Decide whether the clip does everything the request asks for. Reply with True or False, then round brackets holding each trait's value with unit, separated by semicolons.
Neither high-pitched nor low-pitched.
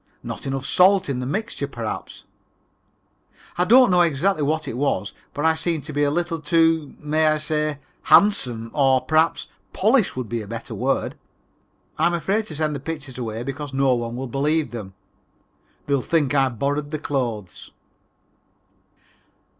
True (145 Hz)